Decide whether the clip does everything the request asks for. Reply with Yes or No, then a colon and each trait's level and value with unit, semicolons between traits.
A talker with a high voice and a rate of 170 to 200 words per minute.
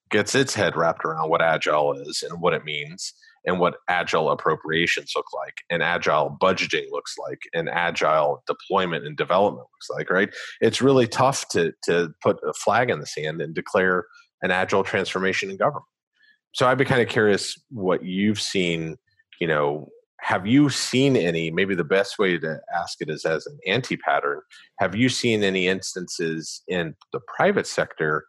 Yes: very high, 350 Hz; average, 180 wpm